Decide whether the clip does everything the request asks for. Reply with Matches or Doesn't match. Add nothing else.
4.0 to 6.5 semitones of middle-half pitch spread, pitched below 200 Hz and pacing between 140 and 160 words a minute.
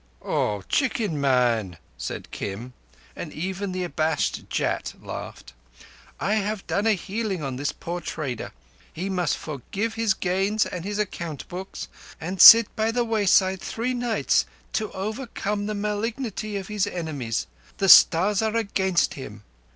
Matches